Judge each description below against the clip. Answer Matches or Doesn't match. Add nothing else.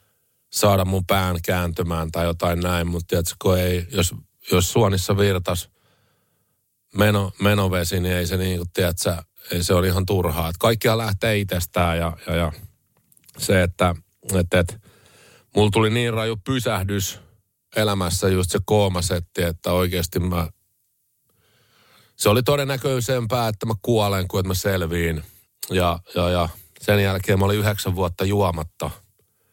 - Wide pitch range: Doesn't match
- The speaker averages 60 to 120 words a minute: Doesn't match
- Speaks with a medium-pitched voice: Doesn't match